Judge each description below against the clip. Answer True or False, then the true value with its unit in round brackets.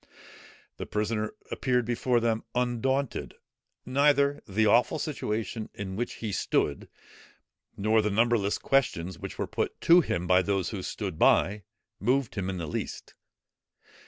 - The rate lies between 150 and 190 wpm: False (140 wpm)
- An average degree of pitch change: True (4.1 semitones)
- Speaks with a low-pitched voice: True (110 Hz)